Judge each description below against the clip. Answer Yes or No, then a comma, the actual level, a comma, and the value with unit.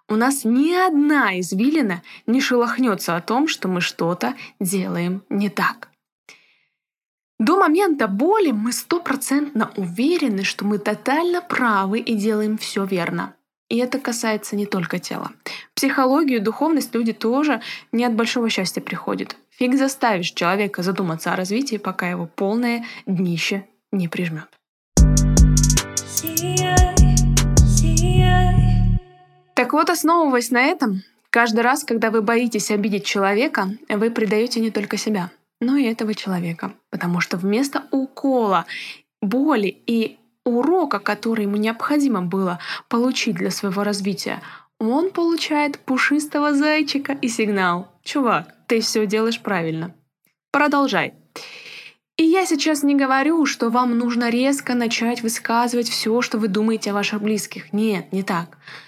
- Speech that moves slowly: No, average, 130 wpm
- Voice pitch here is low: No, high, 225 Hz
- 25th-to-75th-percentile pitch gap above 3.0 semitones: Yes, average, 5.1 semitones